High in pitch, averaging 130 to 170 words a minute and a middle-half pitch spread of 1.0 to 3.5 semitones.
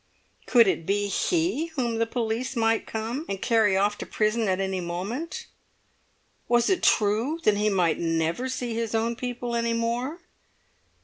Yes: high, 225 Hz; average, 165 wpm; average, 3.2 semitones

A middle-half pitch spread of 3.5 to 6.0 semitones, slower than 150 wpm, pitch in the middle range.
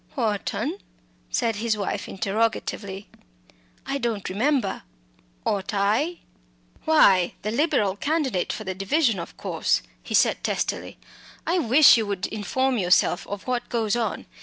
No: average, 4.8 semitones; slow, 135 wpm; high, 220 Hz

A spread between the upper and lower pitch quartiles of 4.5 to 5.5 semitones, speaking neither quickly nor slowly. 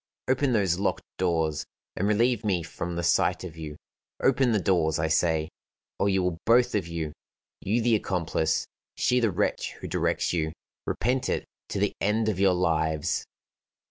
Yes: average, 5.1 semitones; average, 175 wpm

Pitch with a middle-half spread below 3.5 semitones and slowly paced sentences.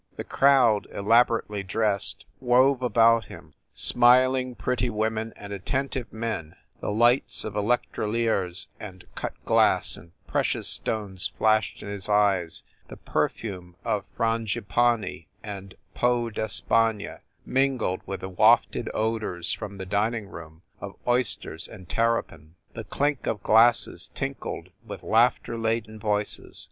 Yes: average, 3.0 semitones; slow, 130 wpm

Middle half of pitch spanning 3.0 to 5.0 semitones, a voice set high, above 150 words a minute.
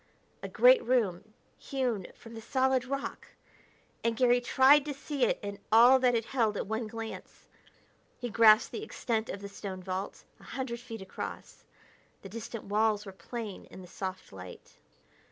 Yes: average, 3.9 semitones; high, 225 Hz; average, 170 wpm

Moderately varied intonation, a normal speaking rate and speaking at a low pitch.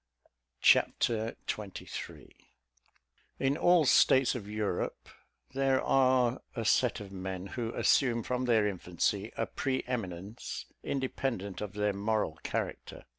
No: average, 4.3 semitones; slow, 120 wpm; low, 115 Hz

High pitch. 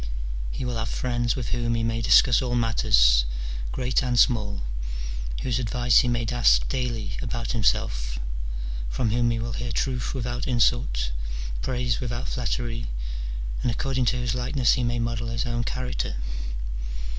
No: low, 120 Hz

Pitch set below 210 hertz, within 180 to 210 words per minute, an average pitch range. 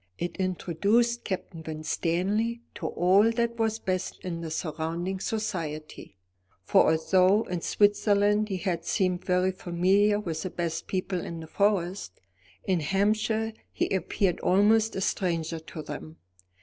No: medium, 185 Hz; slow, 135 wpm; average, 3.6 semitones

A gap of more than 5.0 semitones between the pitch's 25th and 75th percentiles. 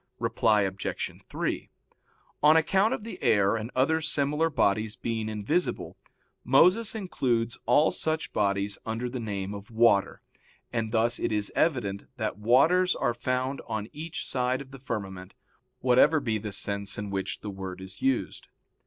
Yes: wide, 5.5 semitones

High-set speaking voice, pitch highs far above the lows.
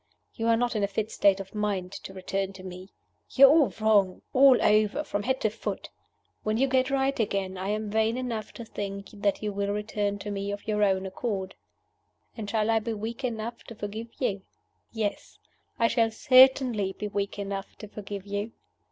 No: high, 210 Hz; narrow, 2.4 semitones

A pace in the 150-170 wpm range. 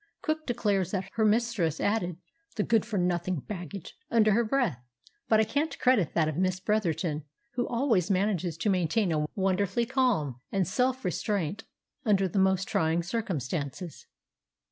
Yes: average, 155 wpm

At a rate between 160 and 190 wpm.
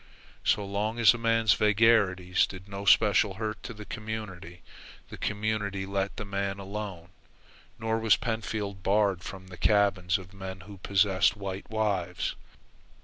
No: average, 145 wpm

